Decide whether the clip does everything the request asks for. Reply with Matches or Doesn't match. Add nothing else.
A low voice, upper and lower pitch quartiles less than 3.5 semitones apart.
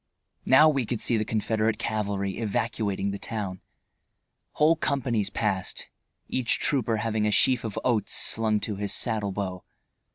Matches